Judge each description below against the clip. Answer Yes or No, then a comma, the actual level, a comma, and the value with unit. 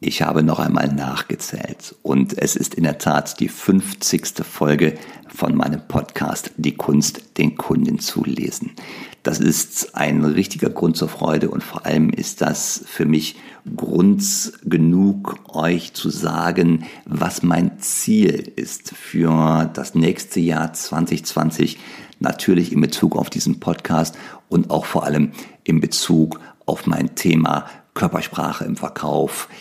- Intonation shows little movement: No, average, 4.1 semitones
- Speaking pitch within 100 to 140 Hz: No, very low, 80 Hz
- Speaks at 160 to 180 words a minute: No, average, 140 wpm